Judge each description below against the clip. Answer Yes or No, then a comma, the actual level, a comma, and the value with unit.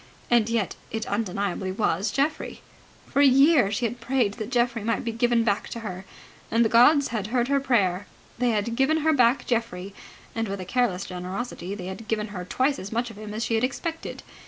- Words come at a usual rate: No, fast, 210 wpm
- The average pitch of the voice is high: Yes, high, 230 Hz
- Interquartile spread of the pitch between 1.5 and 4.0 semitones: Yes, average, 3.6 semitones